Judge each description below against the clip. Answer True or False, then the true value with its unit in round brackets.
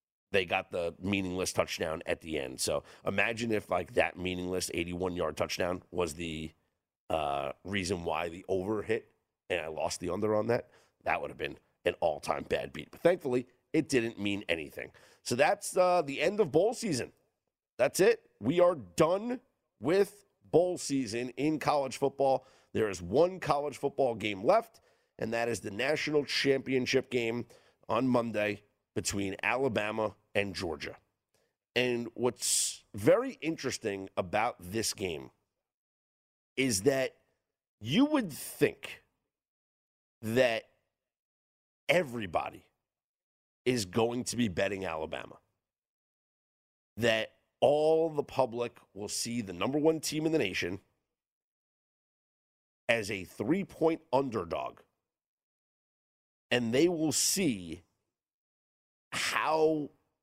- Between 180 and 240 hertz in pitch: False (120 Hz)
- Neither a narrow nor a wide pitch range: False (6.8 semitones)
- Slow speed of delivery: True (125 wpm)